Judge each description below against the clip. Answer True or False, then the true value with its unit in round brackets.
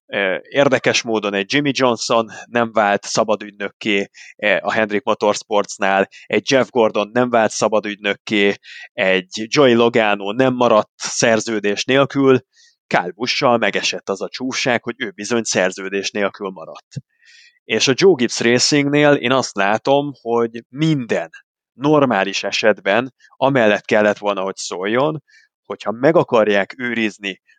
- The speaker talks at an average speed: True (125 wpm)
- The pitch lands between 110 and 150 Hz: True (115 Hz)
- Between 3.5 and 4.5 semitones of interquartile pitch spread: True (4.2 semitones)